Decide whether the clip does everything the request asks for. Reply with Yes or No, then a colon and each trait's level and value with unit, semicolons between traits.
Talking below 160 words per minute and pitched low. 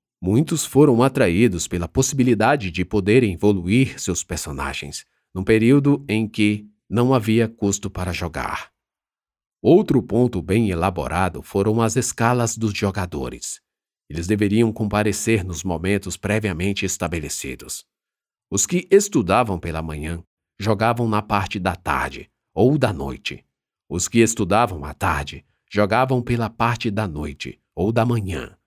Yes: average, 130 wpm; low, 105 Hz